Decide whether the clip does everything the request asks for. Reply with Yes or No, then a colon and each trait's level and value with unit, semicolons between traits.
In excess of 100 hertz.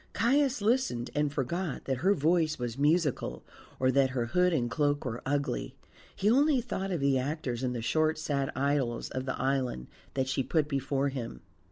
Yes: medium, 140 Hz